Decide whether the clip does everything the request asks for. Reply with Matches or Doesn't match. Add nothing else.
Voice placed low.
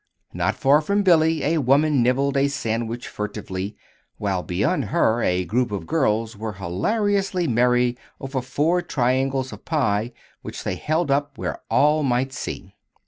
Matches